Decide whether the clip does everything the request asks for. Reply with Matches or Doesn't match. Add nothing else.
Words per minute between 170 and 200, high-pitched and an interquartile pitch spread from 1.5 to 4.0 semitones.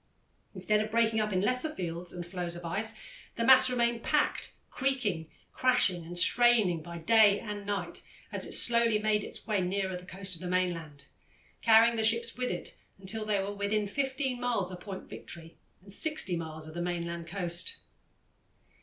Doesn't match